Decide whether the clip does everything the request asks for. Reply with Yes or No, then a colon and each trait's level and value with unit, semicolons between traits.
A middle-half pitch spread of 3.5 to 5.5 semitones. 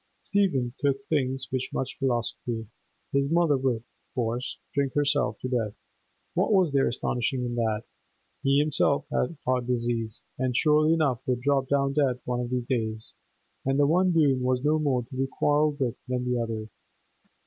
No: average, 2.8 semitones